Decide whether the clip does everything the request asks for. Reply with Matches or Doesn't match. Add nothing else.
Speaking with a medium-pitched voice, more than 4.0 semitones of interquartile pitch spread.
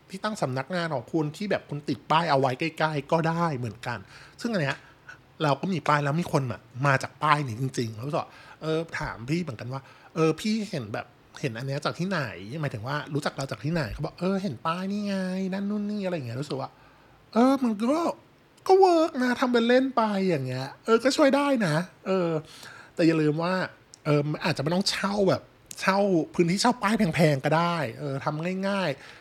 Matches